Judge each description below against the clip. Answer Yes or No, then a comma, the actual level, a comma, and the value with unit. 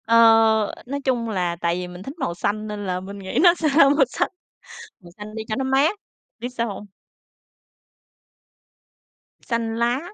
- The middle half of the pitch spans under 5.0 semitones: No, wide, 5.5 semitones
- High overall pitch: Yes, high, 230 Hz